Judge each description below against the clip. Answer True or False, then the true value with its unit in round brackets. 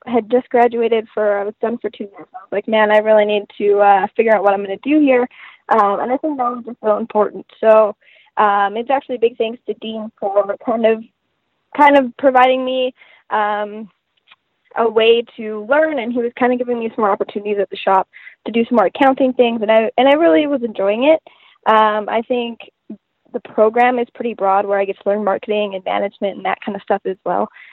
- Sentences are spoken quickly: True (225 wpm)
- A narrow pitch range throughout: False (3.1 semitones)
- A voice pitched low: False (225 Hz)